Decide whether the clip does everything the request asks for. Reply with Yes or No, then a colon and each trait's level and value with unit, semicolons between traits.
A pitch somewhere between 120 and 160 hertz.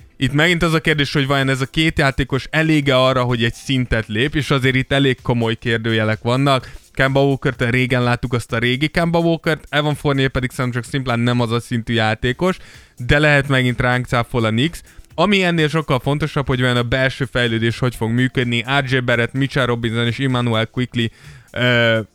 Yes: low, 130 Hz